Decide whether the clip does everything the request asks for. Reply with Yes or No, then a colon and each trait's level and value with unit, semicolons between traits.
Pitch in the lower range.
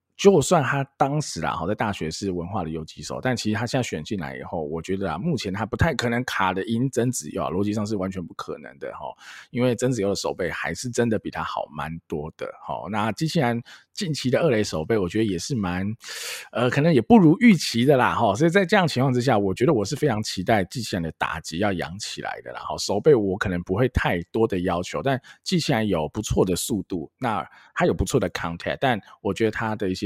Yes: low, 110 Hz